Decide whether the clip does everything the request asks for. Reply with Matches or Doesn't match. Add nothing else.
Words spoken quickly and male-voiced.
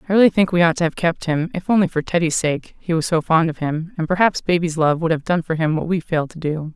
Doesn't match